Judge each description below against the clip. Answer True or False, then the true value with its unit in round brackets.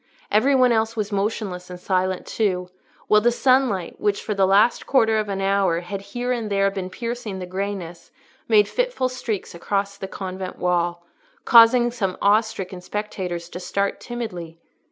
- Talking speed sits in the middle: True (170 wpm)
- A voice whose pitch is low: False (200 Hz)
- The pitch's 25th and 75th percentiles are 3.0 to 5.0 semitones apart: True (3.5 semitones)